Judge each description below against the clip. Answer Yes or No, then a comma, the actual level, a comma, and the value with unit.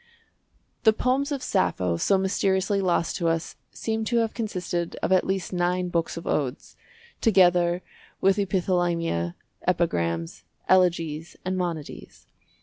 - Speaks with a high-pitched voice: No, medium, 180 Hz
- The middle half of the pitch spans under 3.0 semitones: Yes, narrow, 2.6 semitones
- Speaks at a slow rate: Yes, slow, 130 wpm